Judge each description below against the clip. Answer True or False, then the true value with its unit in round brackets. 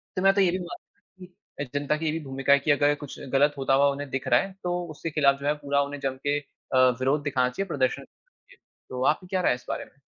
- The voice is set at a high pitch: False (145 Hz)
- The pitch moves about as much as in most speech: True (4.5 semitones)